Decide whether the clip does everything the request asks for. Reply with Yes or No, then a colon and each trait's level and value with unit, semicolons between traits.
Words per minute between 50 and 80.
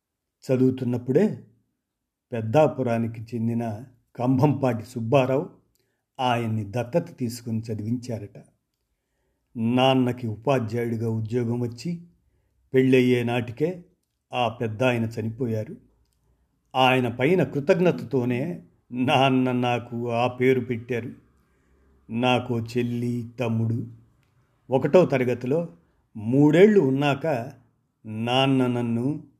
Yes: average, 75 wpm